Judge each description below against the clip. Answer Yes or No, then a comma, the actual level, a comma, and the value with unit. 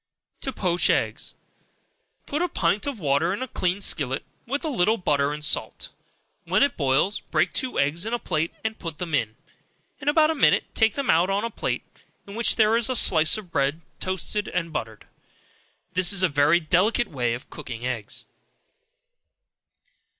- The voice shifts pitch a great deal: Yes, wide, 7.2 semitones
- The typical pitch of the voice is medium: Yes, medium, 180 Hz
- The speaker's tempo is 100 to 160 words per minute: No, average, 180 wpm